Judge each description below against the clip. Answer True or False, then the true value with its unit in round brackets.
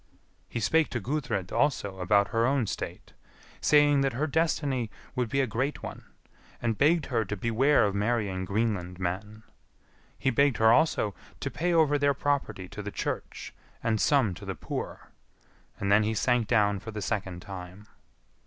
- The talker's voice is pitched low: True (115 Hz)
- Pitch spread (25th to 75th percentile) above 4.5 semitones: True (5.5 semitones)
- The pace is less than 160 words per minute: False (170 wpm)